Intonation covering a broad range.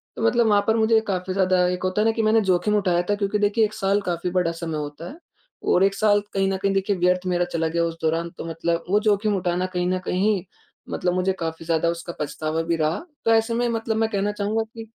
No: average, 3.6 semitones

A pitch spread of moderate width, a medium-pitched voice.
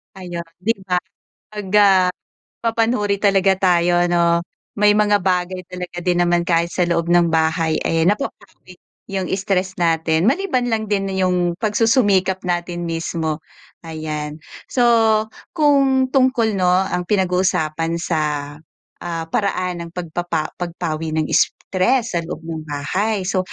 Yes: average, 3.2 semitones; medium, 180 Hz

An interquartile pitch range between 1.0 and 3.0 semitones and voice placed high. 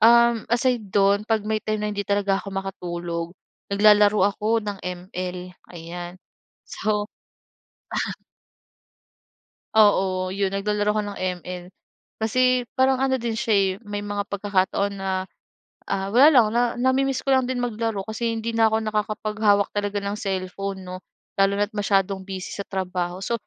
Yes: narrow, 2.5 semitones; high, 205 Hz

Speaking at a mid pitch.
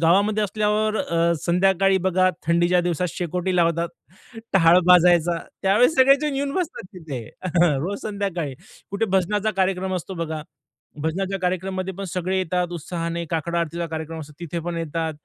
Yes: medium, 180 Hz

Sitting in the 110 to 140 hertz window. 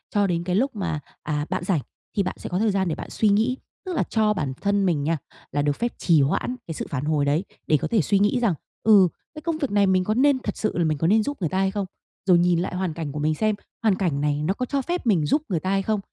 No: high, 190 Hz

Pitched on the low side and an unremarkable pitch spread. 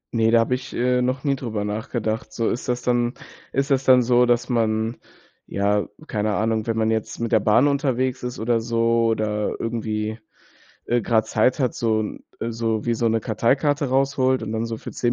No: low, 115 Hz; narrow, 2.2 semitones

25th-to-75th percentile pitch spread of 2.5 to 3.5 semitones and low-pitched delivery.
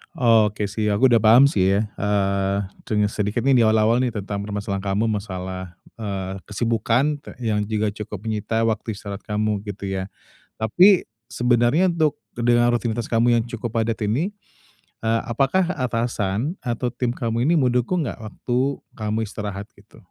Yes: average, 2.8 semitones; low, 110 Hz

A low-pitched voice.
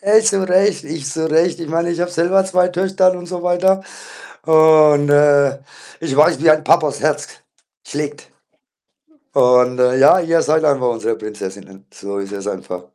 No: medium, 155 Hz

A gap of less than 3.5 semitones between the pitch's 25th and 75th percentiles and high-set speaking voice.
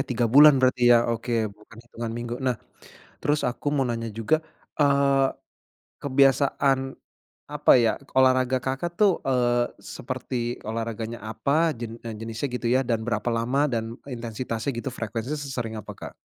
No: average, 2.8 semitones; low, 120 Hz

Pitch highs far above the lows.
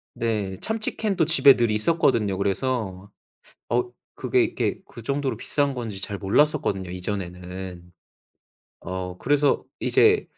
Yes: wide, 6.7 semitones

